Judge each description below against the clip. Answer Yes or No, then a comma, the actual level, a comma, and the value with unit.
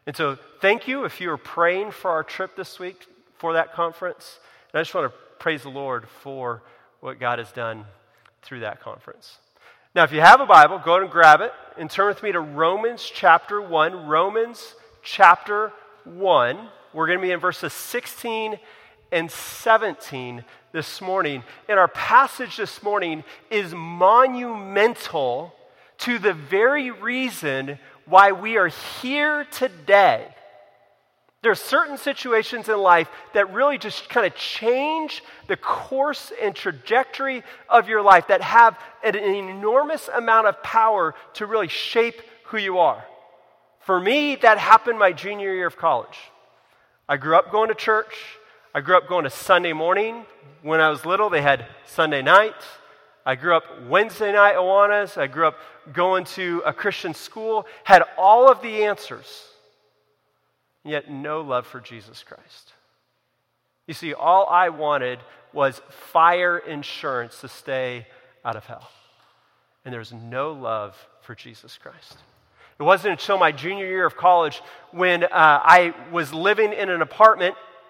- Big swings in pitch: Yes, wide, 5.8 semitones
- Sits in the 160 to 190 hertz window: Yes, medium, 185 Hz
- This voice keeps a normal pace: Yes, average, 160 wpm